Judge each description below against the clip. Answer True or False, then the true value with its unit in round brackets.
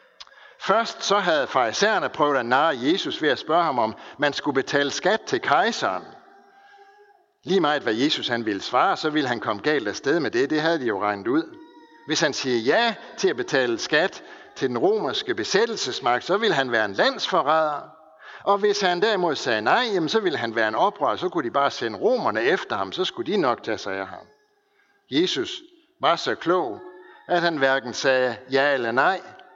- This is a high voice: True (230 Hz)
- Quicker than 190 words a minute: True (200 wpm)